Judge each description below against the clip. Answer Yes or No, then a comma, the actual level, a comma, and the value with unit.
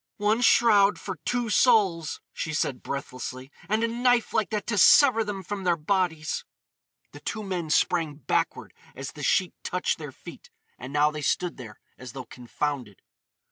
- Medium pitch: Yes, medium, 180 Hz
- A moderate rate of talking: Yes, average, 170 wpm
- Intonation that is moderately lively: No, wide, 6.6 semitones